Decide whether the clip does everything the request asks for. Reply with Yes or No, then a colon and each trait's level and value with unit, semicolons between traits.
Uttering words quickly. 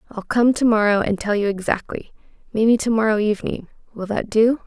No: average, 165 wpm